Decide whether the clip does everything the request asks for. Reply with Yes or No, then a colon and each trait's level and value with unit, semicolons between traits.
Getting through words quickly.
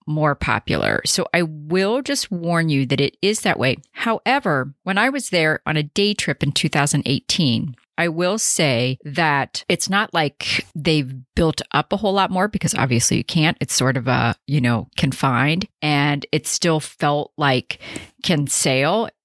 No: average, 175 wpm